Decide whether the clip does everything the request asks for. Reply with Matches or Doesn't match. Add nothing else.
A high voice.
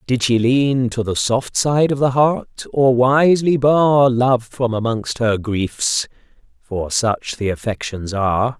Doesn't match